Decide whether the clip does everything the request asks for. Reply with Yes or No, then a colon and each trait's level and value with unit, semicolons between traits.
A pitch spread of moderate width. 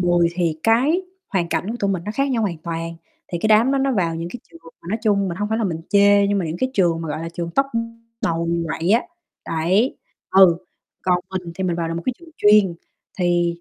Yes: average, 4.3 semitones